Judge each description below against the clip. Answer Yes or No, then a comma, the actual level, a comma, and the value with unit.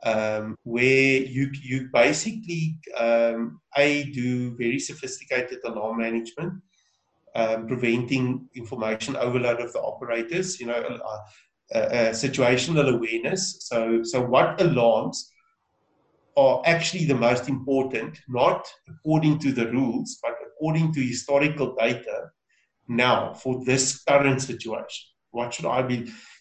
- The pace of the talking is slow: Yes, slow, 125 wpm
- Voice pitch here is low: Yes, low, 130 Hz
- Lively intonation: No, average, 4.2 semitones